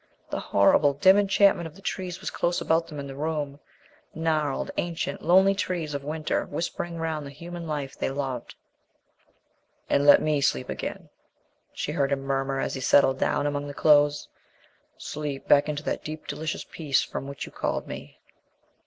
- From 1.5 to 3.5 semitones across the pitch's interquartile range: Yes, average, 2.7 semitones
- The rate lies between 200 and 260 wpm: No, average, 175 wpm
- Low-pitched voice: No, medium, 150 Hz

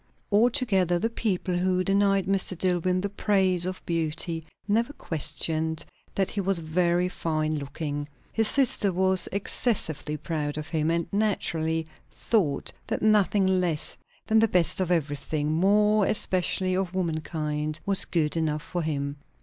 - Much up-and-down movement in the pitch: No, average, 3.7 semitones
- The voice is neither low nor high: Yes, medium, 180 Hz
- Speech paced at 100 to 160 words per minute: Yes, average, 140 wpm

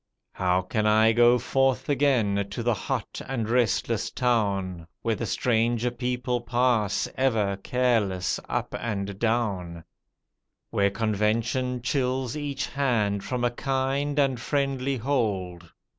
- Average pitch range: Yes, average, 3.9 semitones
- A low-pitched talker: Yes, low, 120 Hz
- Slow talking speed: Yes, slow, 125 wpm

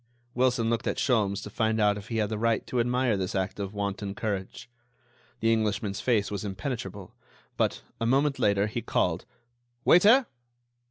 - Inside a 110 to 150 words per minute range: No, average, 170 wpm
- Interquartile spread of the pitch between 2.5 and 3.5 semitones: Yes, average, 3.1 semitones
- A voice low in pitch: Yes, low, 110 Hz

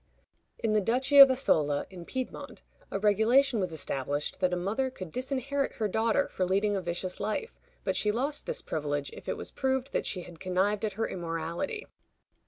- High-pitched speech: Yes, high, 210 Hz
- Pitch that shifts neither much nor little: No, wide, 6.6 semitones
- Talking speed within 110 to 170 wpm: No, average, 190 wpm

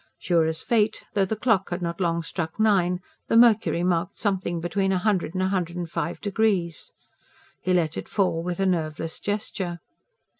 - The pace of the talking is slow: No, average, 185 wpm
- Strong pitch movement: No, average, 2.9 semitones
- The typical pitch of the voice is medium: Yes, medium, 180 Hz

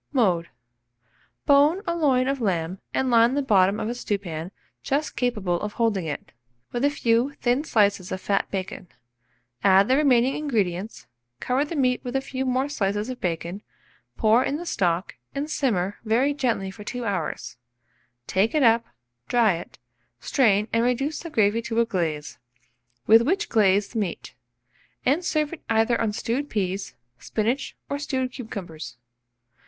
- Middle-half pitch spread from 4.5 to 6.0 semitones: Yes, wide, 5.4 semitones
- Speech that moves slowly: No, average, 160 wpm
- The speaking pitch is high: Yes, high, 230 Hz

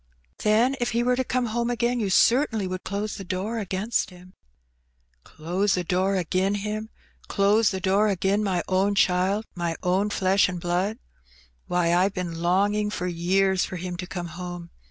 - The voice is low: No, high, 190 Hz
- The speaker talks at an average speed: Yes, average, 180 wpm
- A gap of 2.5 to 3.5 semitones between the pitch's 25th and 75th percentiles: Yes, average, 2.8 semitones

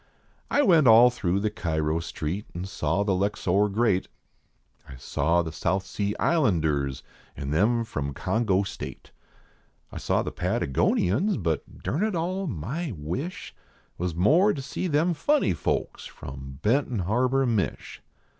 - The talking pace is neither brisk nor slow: Yes, average, 145 wpm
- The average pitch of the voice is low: Yes, low, 100 Hz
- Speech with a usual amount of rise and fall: No, wide, 8.5 semitones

